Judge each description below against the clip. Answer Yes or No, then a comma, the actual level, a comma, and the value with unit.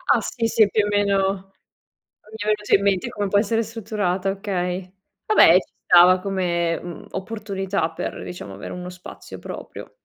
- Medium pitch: No, high, 195 Hz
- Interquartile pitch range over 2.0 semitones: Yes, narrow, 2.6 semitones